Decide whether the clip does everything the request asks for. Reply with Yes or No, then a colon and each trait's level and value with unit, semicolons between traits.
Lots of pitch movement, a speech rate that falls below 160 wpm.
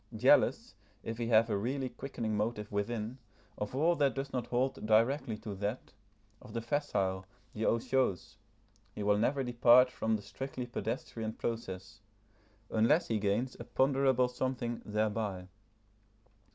No: average, 3.4 semitones; average, 140 wpm